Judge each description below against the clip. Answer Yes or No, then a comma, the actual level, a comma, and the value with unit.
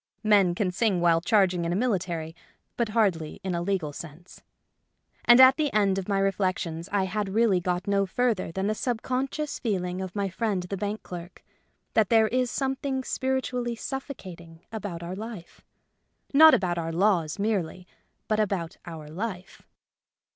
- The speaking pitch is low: No, high, 195 Hz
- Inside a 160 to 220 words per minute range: Yes, average, 165 wpm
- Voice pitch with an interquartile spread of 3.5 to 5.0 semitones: Yes, average, 4.2 semitones